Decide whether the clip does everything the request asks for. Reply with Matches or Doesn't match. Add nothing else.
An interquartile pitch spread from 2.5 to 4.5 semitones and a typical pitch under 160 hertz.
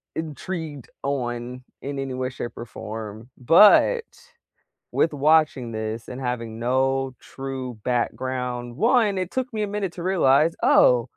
Doesn't match